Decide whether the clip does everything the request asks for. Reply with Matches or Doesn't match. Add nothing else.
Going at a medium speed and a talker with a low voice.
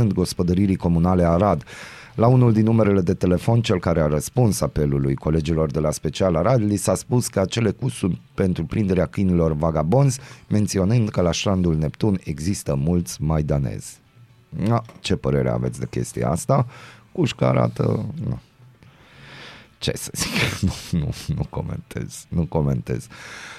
Matches